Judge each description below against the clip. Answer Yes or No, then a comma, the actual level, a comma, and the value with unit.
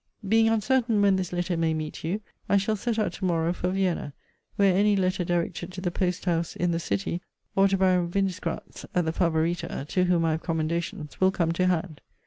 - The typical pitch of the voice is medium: Yes, medium, 180 Hz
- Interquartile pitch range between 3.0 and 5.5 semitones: No, narrow, 2.6 semitones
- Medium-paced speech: No, fast, 210 wpm